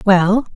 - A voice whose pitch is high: Yes, high, 200 Hz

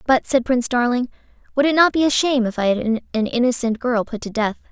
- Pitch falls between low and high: No, high, 245 Hz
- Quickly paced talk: Yes, fast, 240 wpm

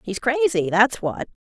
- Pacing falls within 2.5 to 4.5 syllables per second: Yes, 4.2 syllables/s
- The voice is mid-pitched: No, high, 240 Hz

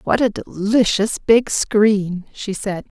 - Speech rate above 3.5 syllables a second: No, 3.3 syllables/s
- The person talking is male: No, female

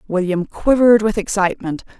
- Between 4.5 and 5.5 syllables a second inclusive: No, 5.8 syllables/s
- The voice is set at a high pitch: Yes, high, 200 Hz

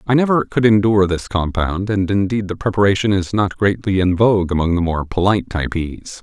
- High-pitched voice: No, low, 100 Hz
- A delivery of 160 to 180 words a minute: No, average, 195 wpm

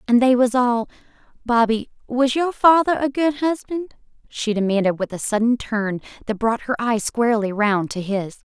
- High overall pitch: Yes, high, 240 Hz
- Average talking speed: Yes, average, 175 wpm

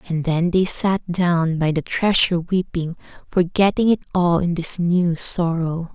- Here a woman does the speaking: Yes, female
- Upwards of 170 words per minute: No, average, 160 wpm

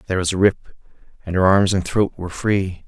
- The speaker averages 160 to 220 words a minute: No, fast, 230 wpm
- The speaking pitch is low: Yes, very low, 95 Hz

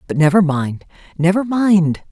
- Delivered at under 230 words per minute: Yes, average, 140 wpm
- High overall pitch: No, medium, 180 Hz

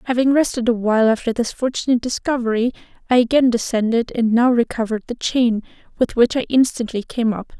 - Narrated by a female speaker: Yes, female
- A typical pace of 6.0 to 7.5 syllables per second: Yes, 6.1 syllables/s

